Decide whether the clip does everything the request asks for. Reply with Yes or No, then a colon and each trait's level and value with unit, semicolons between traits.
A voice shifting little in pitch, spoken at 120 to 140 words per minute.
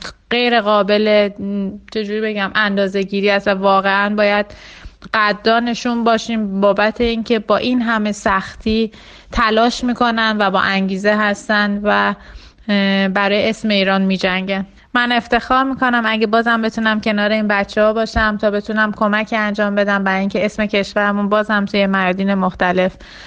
Yes: narrow, 1.9 semitones; average, 135 wpm